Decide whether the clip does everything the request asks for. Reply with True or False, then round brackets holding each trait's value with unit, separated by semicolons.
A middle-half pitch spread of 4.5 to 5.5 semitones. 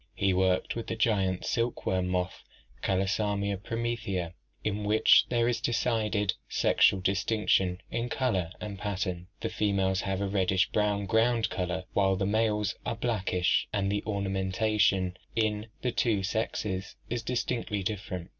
False (2.7 semitones)